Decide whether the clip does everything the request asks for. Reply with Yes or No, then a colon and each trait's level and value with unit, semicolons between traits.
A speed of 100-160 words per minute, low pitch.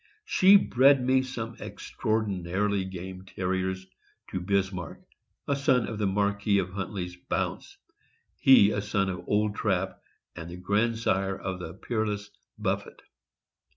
Yes: average, 140 wpm; low, 100 Hz